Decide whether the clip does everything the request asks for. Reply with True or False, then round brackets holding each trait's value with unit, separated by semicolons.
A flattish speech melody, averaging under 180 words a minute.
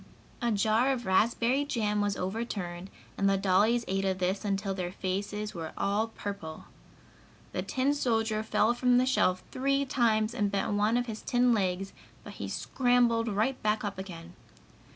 False (3.6 semitones; 170 wpm)